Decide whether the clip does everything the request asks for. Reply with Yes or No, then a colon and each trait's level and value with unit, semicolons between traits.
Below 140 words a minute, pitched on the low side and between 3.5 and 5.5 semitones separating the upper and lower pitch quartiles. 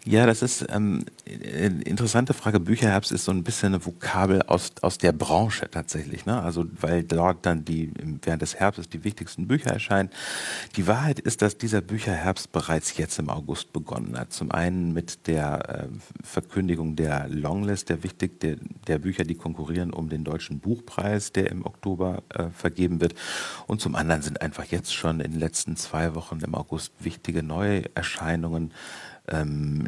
No: average, 175 wpm; very low, 90 Hz; average, 3.8 semitones